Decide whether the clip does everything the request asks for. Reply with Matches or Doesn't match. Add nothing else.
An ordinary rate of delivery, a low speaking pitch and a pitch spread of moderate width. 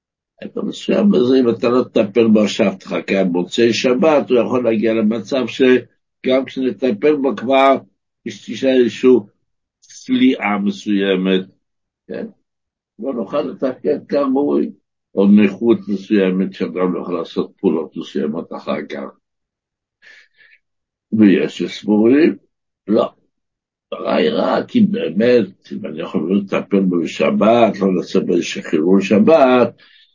Matches